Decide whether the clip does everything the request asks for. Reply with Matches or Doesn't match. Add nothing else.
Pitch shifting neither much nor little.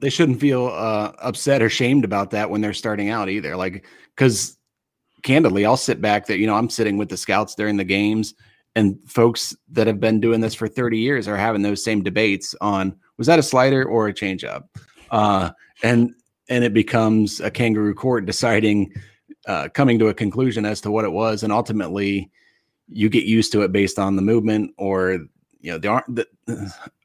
Doesn't match